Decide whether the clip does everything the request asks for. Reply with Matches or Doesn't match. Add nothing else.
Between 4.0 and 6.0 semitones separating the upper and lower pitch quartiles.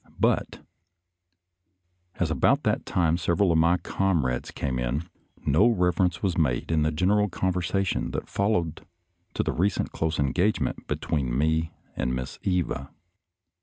Doesn't match